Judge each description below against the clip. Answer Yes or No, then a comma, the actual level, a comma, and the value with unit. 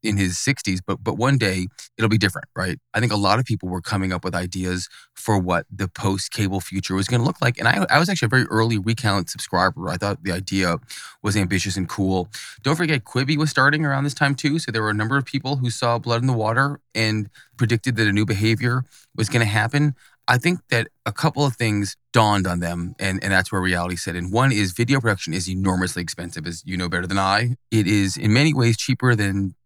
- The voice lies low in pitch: Yes, low, 110 Hz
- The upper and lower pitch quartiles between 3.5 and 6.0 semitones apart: Yes, average, 4.8 semitones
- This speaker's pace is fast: Yes, fast, 240 wpm